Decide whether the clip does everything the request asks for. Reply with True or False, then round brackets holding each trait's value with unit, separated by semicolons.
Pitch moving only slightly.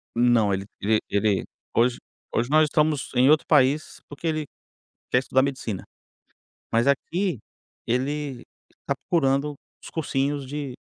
False (3.8 semitones)